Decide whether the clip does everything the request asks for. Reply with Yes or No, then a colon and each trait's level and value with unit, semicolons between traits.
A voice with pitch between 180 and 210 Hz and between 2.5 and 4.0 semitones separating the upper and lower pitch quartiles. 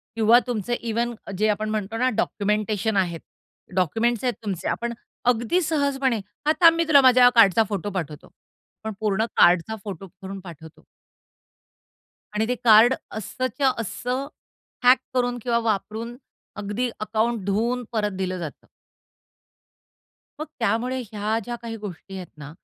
No: high, 220 Hz; average, 3.5 semitones